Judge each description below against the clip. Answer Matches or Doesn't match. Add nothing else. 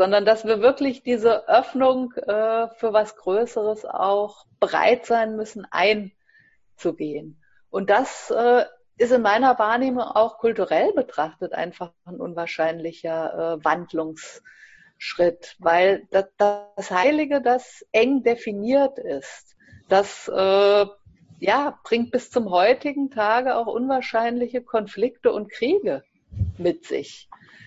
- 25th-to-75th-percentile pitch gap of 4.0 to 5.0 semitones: Matches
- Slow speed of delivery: Matches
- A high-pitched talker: Matches